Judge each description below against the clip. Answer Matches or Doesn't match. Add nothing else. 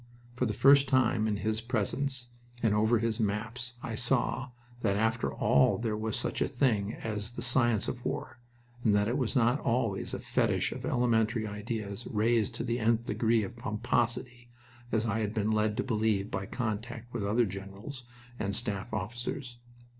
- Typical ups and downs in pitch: Doesn't match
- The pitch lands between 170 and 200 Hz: Doesn't match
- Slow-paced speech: Doesn't match